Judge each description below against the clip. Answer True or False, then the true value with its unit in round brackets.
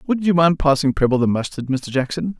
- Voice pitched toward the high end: False (150 Hz)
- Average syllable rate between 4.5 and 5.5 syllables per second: False (5.8 syllables/s)